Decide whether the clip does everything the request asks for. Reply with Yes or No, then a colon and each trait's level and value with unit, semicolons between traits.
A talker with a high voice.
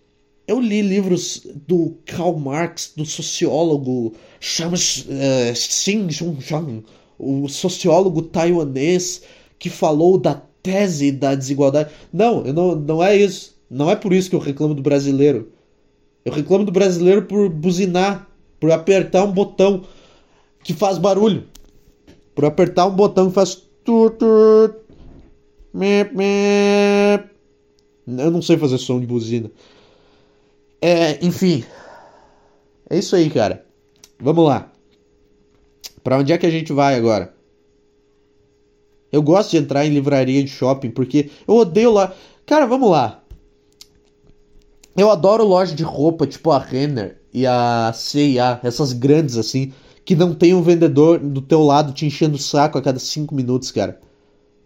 No: medium, 155 Hz